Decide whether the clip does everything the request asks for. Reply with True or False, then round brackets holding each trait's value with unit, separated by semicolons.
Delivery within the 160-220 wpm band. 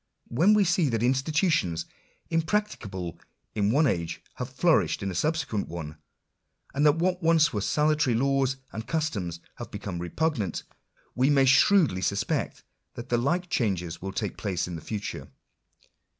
False (150 wpm)